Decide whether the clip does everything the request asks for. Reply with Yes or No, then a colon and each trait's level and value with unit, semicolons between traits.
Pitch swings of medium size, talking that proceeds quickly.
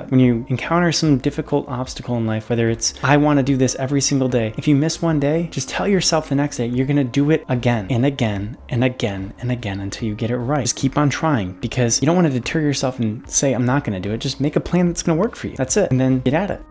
Yes: average, 3.4 semitones; fast, 295 wpm